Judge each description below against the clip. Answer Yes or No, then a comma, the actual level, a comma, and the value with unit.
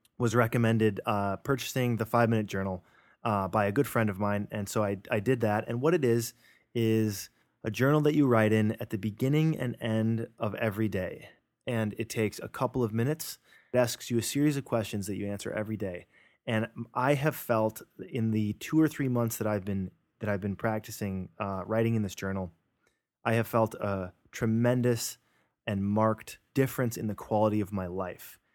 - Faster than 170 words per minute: Yes, average, 200 wpm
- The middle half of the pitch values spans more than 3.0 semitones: No, average, 2.7 semitones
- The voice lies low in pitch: Yes, low, 110 Hz